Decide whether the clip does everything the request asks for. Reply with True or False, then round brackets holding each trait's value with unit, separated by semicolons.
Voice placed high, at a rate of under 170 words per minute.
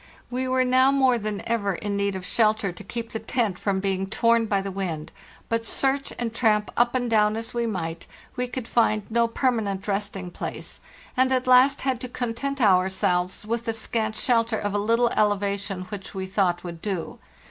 False (215 Hz; 200 wpm)